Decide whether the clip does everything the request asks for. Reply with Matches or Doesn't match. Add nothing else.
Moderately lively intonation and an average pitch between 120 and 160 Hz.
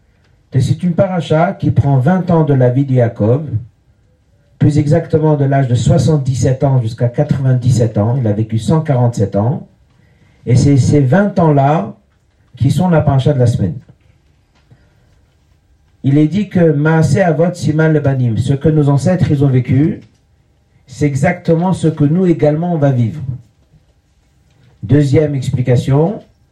Matches